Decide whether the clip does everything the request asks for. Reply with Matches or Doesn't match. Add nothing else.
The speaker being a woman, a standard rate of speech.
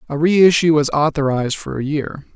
Doesn't match